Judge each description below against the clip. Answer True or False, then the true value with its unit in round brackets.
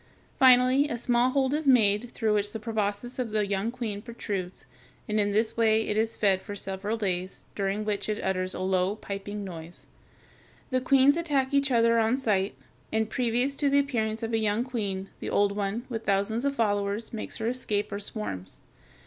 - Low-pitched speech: False (220 Hz)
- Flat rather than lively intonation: False (3.3 semitones)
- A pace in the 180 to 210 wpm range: True (190 wpm)